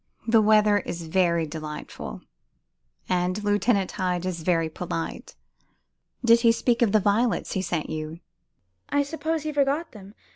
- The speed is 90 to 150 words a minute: Yes, average, 145 wpm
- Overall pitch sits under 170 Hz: No, high, 200 Hz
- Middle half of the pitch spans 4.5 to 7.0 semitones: Yes, average, 5.3 semitones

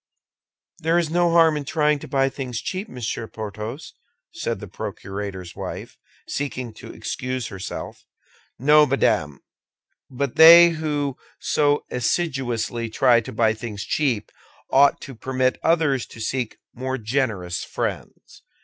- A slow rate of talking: Yes, slow, 130 wpm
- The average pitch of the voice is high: No, low, 130 Hz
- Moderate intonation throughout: Yes, average, 4.9 semitones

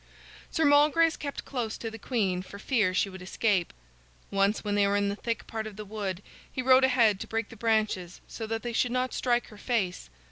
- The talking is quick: Yes, fast, 220 wpm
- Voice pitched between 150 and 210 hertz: No, high, 220 Hz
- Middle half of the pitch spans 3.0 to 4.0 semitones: Yes, average, 3.5 semitones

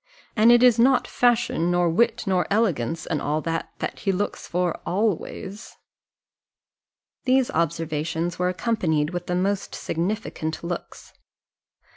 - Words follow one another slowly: Yes, slow, 130 wpm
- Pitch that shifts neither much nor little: Yes, average, 4.9 semitones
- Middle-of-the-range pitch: Yes, medium, 180 Hz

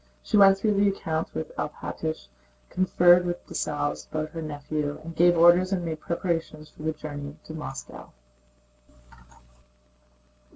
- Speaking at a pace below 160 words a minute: Yes, slow, 135 wpm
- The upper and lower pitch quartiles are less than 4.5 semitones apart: Yes, average, 2.7 semitones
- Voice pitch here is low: No, medium, 165 Hz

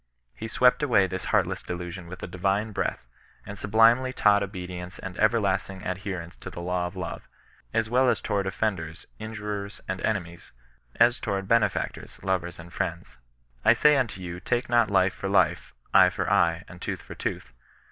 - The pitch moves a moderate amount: Yes, average, 3.5 semitones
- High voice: No, very low, 95 Hz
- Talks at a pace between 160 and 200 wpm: Yes, average, 165 wpm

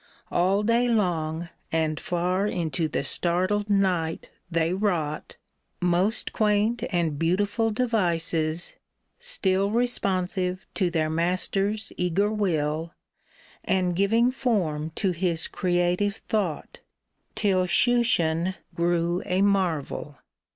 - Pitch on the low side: No, medium, 185 Hz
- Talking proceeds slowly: Yes, slow, 110 wpm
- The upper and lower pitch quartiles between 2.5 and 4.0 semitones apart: Yes, average, 3.5 semitones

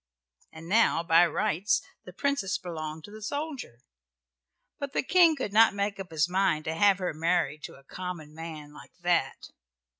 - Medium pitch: Yes, medium, 180 Hz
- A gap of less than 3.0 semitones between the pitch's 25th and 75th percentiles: No, average, 4.6 semitones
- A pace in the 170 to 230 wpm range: Yes, average, 175 wpm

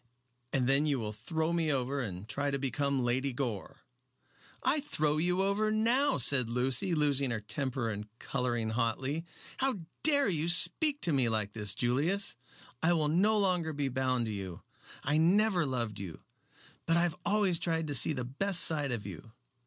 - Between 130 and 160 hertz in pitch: Yes, medium, 140 Hz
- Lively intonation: Yes, wide, 6.0 semitones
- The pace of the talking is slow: No, average, 180 wpm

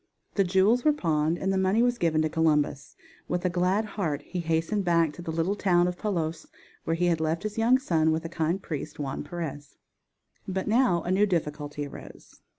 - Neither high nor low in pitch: Yes, medium, 175 Hz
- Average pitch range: Yes, average, 3.4 semitones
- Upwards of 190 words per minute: Yes, fast, 205 wpm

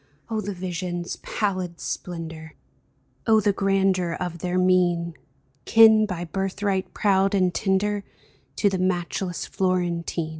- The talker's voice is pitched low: No, medium, 185 Hz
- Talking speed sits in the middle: No, slow, 125 wpm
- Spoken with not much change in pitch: Yes, narrow, 2.1 semitones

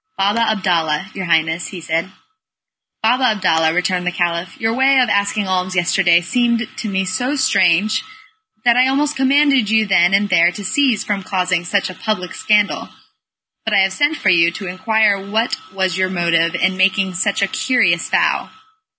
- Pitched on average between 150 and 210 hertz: Yes, high, 190 Hz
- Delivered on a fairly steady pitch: No, average, 3.6 semitones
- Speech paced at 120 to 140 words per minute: No, average, 175 wpm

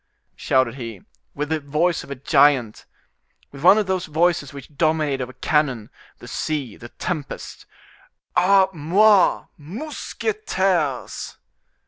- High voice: No, medium, 150 Hz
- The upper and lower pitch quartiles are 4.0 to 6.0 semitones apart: Yes, average, 4.8 semitones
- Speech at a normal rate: No, slow, 120 wpm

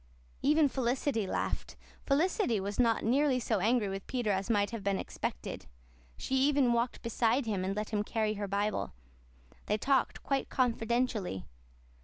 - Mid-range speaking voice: No, high, 230 Hz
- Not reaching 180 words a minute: Yes, average, 155 wpm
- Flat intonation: No, average, 3.9 semitones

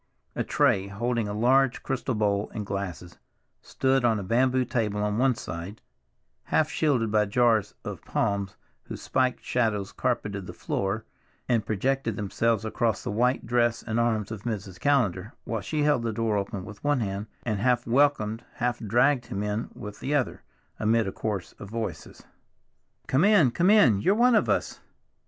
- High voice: No, low, 115 Hz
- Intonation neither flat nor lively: Yes, average, 3.6 semitones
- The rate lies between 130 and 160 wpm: No, average, 175 wpm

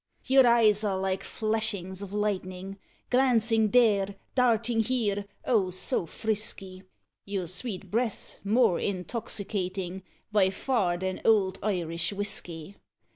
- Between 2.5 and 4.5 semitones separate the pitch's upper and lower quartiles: Yes, average, 2.9 semitones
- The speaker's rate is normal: No, slow, 115 wpm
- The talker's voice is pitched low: No, high, 200 Hz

